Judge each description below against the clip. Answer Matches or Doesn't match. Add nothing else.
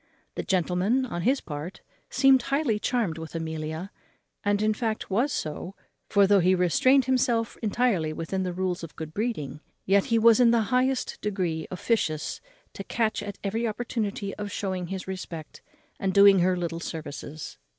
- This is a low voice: Doesn't match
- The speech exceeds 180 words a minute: Doesn't match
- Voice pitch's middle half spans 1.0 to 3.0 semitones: Doesn't match